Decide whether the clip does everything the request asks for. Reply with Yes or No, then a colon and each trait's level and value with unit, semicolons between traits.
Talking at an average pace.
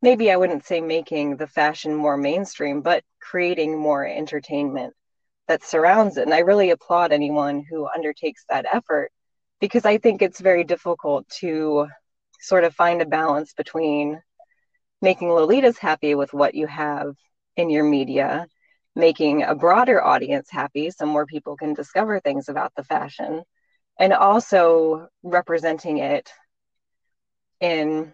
Yes: average, 145 wpm